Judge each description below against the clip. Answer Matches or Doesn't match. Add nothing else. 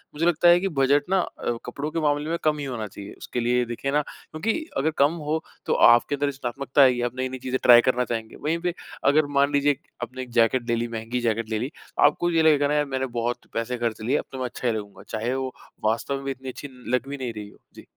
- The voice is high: Doesn't match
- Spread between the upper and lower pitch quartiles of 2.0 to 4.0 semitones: Matches